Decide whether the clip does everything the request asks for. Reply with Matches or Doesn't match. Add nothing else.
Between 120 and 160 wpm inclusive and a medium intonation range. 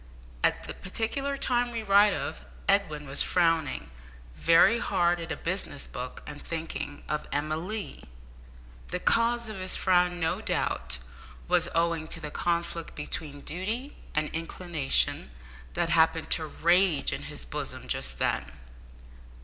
Matches